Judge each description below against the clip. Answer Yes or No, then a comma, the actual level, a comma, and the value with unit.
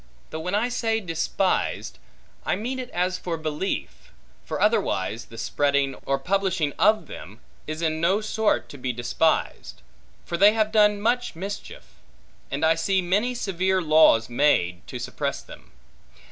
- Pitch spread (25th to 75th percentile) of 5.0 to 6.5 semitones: Yes, wide, 5.4 semitones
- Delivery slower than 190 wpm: Yes, average, 155 wpm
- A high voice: No, medium, 180 Hz